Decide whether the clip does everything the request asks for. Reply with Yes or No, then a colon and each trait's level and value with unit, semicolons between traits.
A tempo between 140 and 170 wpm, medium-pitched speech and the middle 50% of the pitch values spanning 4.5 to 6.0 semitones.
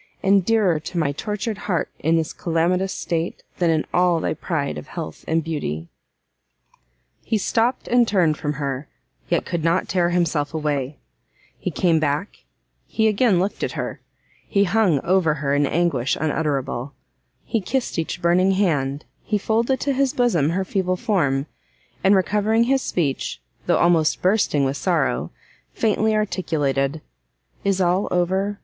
Yes: average, 155 wpm; medium, 175 Hz; average, 4.9 semitones